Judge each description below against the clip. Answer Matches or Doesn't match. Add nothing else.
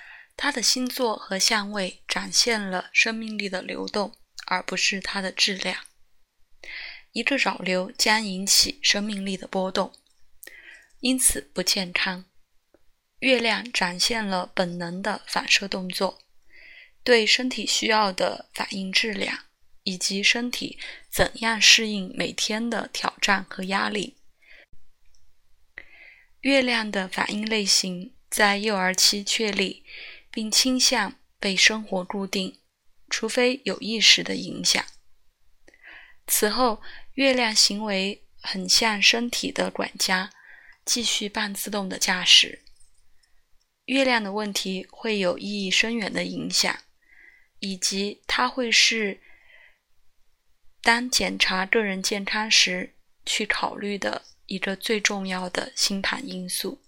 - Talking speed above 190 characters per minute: Doesn't match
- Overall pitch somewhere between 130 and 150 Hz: Doesn't match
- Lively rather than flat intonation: Doesn't match